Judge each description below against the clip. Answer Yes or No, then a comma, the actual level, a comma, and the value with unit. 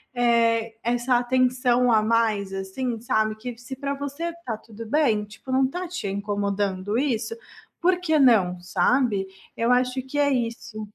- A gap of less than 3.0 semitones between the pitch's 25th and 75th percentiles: No, average, 3.5 semitones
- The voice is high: Yes, high, 240 Hz